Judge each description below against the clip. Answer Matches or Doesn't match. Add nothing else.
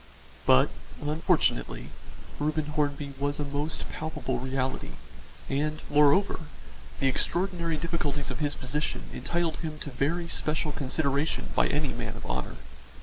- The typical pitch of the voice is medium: Matches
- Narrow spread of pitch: Matches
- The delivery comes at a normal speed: Doesn't match